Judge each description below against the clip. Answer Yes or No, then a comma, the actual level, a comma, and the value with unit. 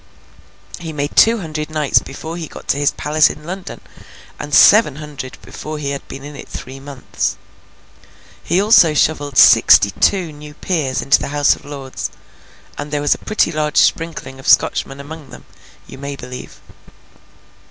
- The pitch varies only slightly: Yes, narrow, 2.3 semitones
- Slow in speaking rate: No, average, 165 wpm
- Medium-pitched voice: Yes, medium, 150 Hz